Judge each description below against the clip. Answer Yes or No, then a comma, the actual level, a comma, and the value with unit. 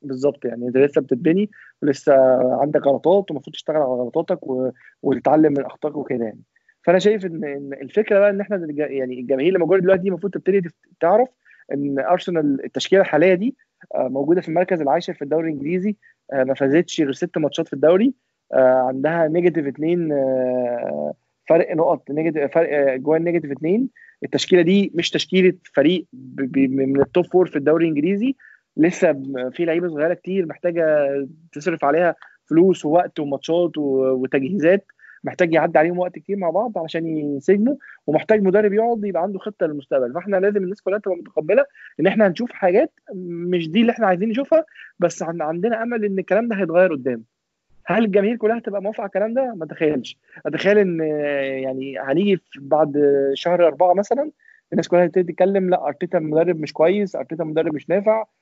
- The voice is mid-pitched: Yes, medium, 170 Hz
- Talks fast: Yes, fast, 160 wpm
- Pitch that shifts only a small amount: No, average, 5.1 semitones